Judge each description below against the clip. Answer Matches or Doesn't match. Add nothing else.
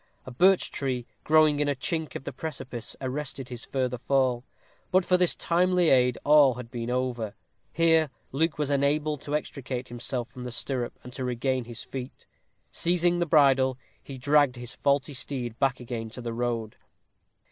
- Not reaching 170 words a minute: Doesn't match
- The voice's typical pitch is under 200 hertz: Matches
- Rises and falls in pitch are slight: Doesn't match